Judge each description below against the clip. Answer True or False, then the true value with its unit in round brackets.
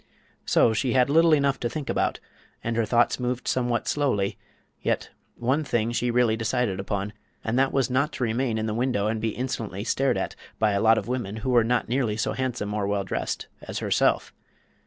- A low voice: True (120 Hz)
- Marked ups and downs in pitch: False (2.9 semitones)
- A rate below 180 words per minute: False (205 wpm)